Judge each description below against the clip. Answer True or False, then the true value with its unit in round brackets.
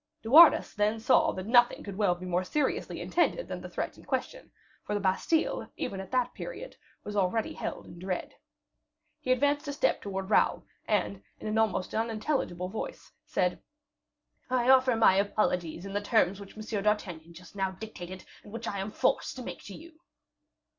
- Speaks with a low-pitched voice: False (210 Hz)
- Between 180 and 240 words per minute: True (185 wpm)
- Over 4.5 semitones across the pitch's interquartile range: True (5.0 semitones)